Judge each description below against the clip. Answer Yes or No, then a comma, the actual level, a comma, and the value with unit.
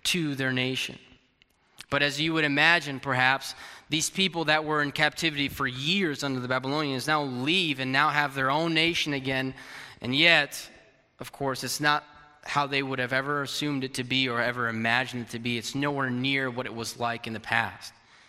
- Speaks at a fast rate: No, average, 195 wpm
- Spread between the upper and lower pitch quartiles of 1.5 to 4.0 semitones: Yes, narrow, 2.6 semitones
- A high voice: No, low, 135 Hz